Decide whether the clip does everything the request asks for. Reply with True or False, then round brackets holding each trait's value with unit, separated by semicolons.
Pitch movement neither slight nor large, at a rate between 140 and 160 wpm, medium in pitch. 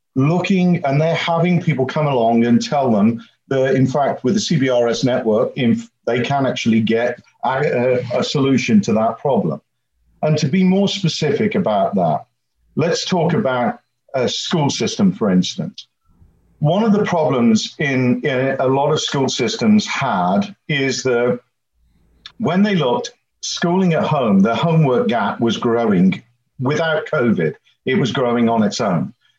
False (7.8 semitones; 155 wpm; 150 Hz)